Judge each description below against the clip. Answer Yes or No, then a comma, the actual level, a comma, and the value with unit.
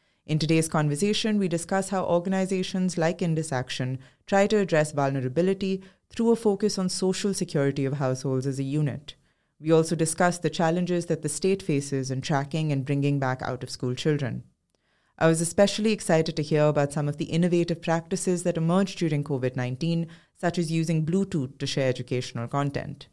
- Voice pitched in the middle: Yes, medium, 160 Hz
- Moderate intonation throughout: Yes, average, 4.6 semitones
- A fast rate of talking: No, average, 170 wpm